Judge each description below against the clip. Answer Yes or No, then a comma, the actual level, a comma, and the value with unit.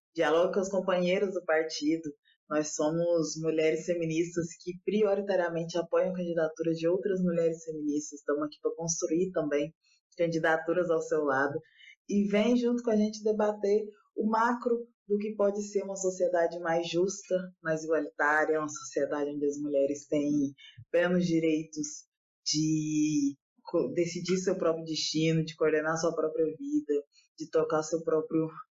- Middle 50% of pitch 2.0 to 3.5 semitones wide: Yes, average, 3.0 semitones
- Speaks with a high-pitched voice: No, medium, 165 Hz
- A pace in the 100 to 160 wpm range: Yes, average, 140 wpm